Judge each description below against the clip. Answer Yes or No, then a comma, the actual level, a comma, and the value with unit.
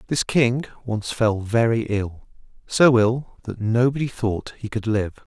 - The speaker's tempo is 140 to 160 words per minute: Yes, average, 145 wpm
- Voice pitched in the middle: No, low, 115 Hz